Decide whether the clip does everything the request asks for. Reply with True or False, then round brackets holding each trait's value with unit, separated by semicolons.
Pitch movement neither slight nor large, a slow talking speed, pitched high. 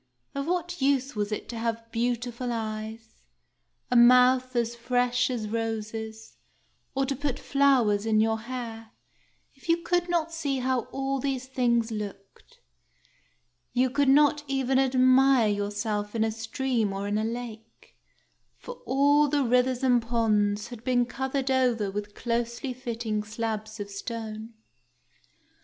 False (3.2 semitones; 145 wpm; 240 Hz)